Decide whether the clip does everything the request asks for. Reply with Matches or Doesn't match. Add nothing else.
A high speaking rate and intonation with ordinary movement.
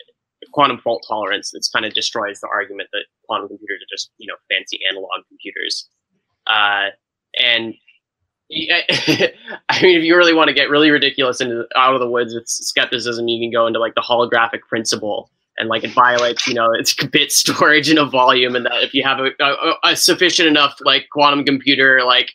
Doesn't match